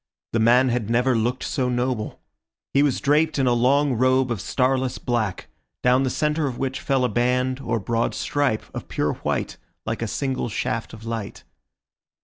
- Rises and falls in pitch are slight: Yes, narrow, 2.2 semitones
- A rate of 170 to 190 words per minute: Yes, average, 180 wpm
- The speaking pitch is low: Yes, low, 125 Hz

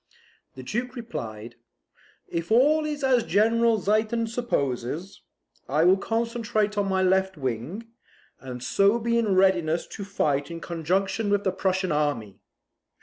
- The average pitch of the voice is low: No, high, 195 Hz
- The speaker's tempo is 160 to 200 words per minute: No, average, 140 wpm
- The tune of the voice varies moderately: No, wide, 6.6 semitones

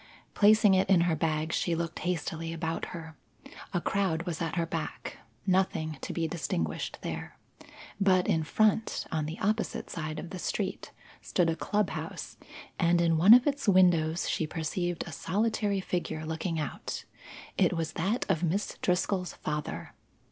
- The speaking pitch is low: No, medium, 170 Hz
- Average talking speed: Yes, average, 160 wpm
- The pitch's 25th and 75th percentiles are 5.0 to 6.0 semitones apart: No, average, 3.0 semitones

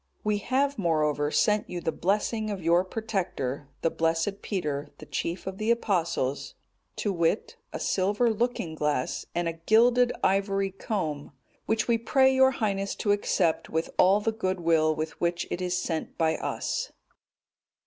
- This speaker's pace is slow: No, average, 160 wpm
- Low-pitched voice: No, high, 190 Hz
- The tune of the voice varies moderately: Yes, average, 4.9 semitones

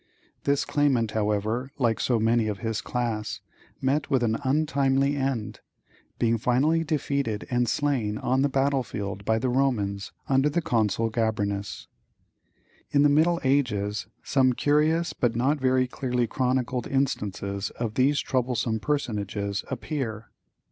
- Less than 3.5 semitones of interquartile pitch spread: No, average, 4.0 semitones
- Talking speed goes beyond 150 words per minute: No, slow, 135 wpm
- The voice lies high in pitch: No, low, 125 Hz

